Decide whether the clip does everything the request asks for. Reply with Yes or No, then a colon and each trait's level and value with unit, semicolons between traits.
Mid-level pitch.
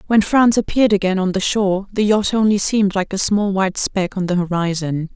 No: high, 195 Hz